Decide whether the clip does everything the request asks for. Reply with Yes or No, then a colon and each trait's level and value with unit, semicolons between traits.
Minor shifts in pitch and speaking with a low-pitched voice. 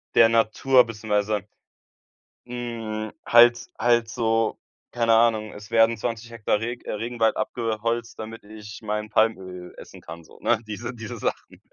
Yes: narrow, 1.6 semitones; low, 115 Hz